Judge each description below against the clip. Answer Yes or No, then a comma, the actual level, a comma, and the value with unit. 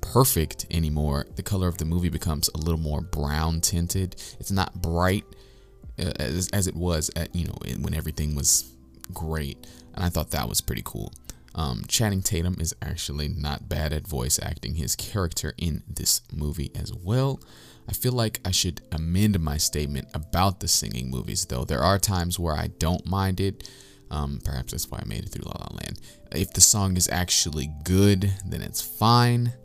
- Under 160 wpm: No, average, 185 wpm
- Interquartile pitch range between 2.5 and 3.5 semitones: No, average, 4.5 semitones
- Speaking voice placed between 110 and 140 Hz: No, very low, 90 Hz